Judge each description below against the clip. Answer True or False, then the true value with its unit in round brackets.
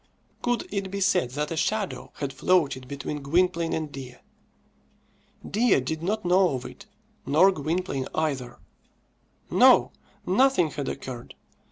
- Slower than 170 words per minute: True (135 wpm)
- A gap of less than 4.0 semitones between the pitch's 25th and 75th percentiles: False (5.3 semitones)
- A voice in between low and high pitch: True (160 Hz)